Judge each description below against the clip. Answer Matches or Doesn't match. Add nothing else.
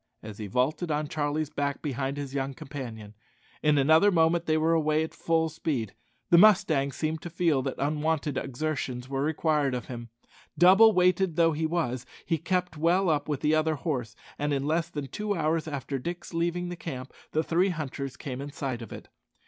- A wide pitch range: Doesn't match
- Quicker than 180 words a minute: Matches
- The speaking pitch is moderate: Matches